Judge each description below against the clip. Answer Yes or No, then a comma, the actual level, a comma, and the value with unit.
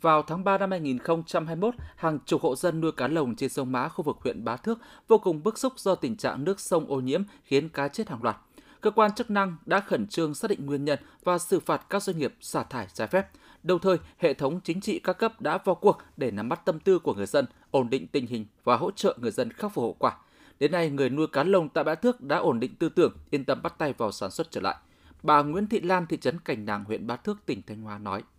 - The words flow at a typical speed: No, fast, 270 wpm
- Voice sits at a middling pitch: Yes, medium, 165 Hz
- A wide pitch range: Yes, wide, 5.8 semitones